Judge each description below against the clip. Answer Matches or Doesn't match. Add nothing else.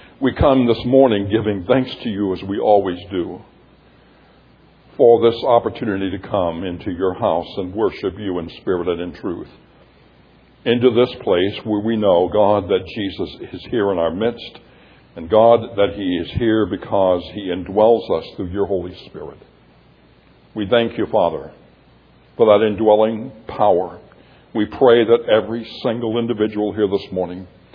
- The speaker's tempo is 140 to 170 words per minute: Matches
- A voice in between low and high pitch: Doesn't match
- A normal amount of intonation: Matches